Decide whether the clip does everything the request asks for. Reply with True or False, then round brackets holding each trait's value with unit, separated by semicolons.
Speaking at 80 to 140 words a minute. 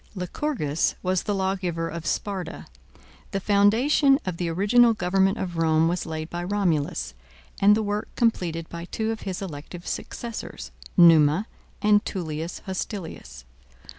True (135 wpm)